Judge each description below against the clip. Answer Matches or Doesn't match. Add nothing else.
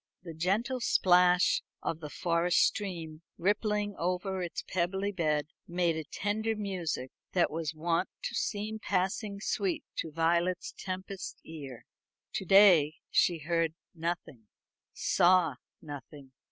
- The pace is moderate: Doesn't match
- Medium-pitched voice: Matches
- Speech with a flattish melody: Doesn't match